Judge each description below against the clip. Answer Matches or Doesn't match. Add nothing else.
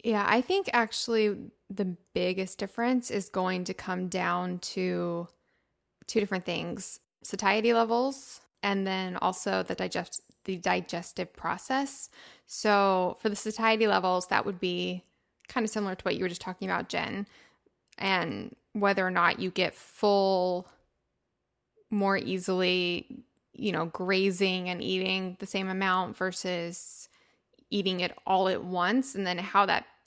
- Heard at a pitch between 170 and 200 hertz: Matches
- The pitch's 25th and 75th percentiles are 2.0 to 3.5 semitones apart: Matches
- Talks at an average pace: Matches